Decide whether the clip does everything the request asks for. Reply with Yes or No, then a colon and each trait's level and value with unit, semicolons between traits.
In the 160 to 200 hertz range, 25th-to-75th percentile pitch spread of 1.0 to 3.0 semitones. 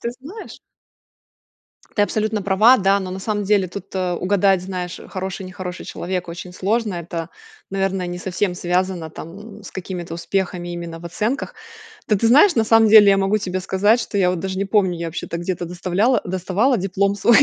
Yes: high, 190 Hz; narrow, 2.6 semitones